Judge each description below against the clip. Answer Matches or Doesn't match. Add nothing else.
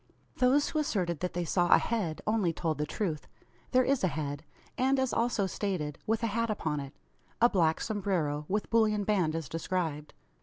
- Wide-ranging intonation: Matches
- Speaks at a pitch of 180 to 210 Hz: Matches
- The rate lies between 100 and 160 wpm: Doesn't match